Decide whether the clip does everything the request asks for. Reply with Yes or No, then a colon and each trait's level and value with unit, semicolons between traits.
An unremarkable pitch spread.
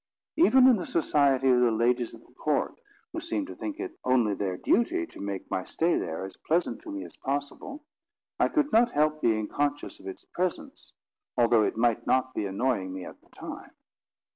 No: wide, 8.8 semitones